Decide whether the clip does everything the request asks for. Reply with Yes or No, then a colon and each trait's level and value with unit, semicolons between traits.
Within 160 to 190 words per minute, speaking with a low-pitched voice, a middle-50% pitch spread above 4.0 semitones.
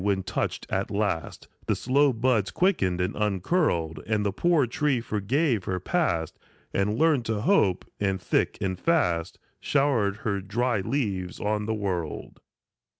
No: average, 150 wpm; low, 105 Hz; wide, 5.5 semitones